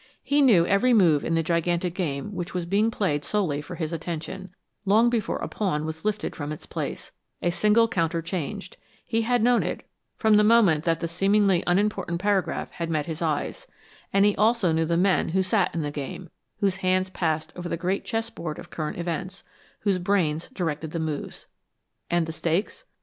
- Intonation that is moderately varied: Yes, average, 4.0 semitones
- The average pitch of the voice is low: No, medium, 180 Hz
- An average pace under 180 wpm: No, average, 195 wpm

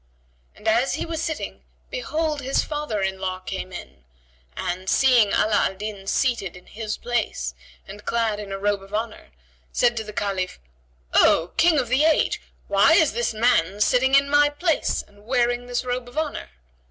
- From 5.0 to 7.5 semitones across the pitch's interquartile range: Yes, average, 5.3 semitones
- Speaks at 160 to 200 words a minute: Yes, average, 180 wpm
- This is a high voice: Yes, high, 230 Hz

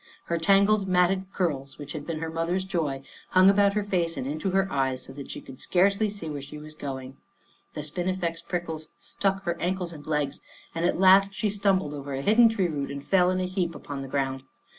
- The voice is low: No, medium, 170 Hz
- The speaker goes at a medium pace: No, fast, 220 wpm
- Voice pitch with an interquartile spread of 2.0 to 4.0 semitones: No, average, 4.7 semitones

